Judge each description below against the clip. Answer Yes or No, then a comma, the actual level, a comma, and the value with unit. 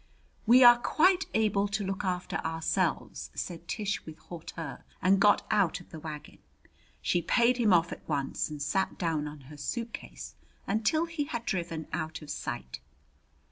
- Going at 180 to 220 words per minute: No, average, 165 wpm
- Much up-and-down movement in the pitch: Yes, wide, 5.7 semitones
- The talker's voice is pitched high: No, medium, 180 Hz